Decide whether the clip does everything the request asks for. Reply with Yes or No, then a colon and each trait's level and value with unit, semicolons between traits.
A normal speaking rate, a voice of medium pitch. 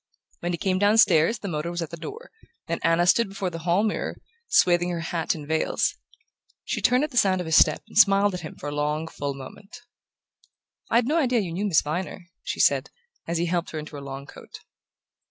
No: fast, 220 wpm; medium, 175 Hz